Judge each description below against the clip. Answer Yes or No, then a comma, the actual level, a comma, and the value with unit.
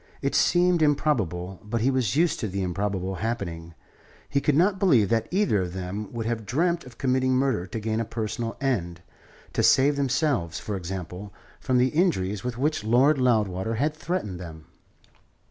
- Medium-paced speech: Yes, average, 175 wpm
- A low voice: Yes, low, 115 Hz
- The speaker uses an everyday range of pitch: No, wide, 6.4 semitones